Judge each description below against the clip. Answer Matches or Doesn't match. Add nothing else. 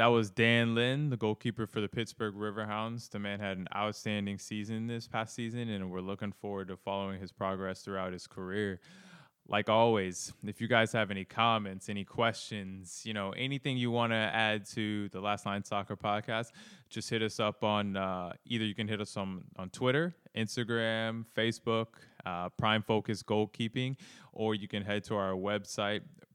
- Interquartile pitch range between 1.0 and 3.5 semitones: Matches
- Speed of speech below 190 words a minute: Matches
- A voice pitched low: Matches